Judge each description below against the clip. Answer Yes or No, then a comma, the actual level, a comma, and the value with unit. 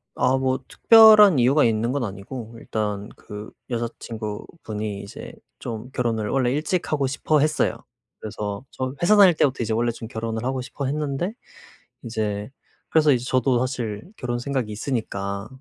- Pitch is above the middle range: No, low, 120 Hz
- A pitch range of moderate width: Yes, average, 4.2 semitones